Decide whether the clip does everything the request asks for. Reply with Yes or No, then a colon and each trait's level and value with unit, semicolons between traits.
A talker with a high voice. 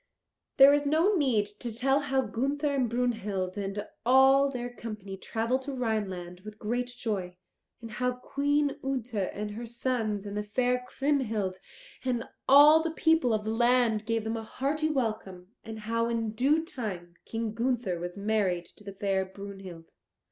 Yes: high, 230 Hz